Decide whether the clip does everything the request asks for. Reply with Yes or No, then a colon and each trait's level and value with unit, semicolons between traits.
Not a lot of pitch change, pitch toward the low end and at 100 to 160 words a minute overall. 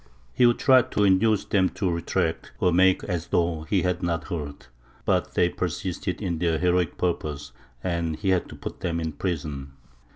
No: narrow, 2.3 semitones; very low, 90 Hz; average, 185 wpm